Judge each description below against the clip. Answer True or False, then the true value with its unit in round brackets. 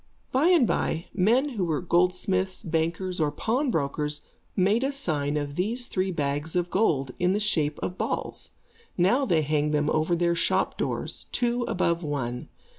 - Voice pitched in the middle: True (175 Hz)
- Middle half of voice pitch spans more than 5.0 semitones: True (5.6 semitones)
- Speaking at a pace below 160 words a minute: False (165 wpm)